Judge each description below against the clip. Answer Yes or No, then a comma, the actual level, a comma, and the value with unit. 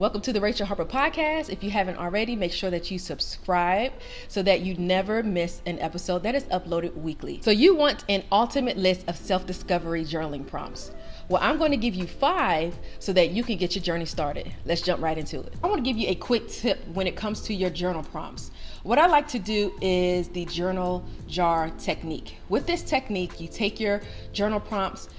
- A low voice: No, medium, 185 Hz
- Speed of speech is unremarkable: No, fast, 215 wpm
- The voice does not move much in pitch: No, average, 3.7 semitones